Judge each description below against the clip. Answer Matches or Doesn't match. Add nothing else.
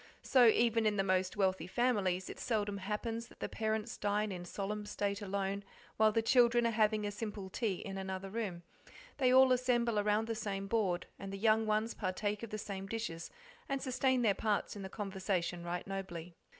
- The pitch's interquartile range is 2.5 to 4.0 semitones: Matches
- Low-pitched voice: Doesn't match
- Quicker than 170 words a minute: Matches